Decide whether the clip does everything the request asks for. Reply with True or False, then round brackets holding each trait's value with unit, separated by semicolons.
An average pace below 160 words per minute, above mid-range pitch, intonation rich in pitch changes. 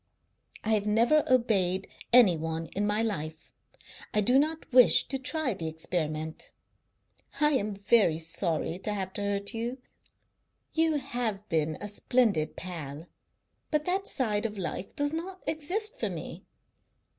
True (140 wpm; 210 Hz; 7.1 semitones)